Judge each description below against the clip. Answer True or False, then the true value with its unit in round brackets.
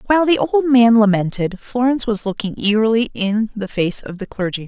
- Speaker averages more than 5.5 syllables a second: True (5.8 syllables/s)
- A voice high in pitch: True (220 Hz)